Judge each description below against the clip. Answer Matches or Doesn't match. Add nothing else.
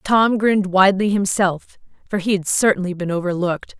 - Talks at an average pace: Matches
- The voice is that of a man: Doesn't match